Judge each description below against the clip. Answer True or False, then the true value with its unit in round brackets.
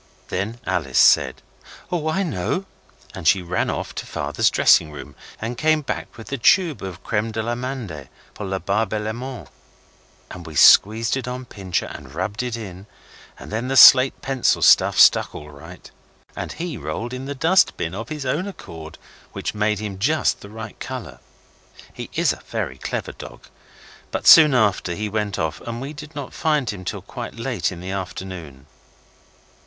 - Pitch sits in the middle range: False (110 Hz)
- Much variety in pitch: True (6.1 semitones)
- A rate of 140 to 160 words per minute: False (180 wpm)